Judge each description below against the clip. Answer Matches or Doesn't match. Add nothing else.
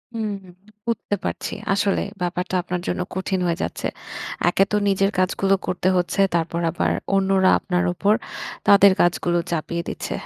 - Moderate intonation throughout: Doesn't match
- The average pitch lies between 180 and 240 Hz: Matches